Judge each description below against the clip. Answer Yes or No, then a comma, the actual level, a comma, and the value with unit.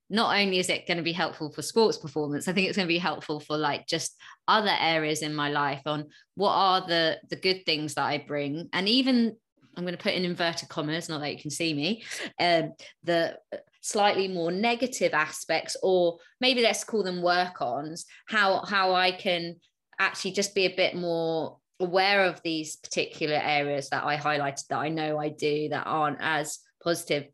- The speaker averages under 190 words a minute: No, average, 200 wpm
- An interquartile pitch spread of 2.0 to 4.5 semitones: Yes, average, 3.7 semitones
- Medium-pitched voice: Yes, medium, 170 Hz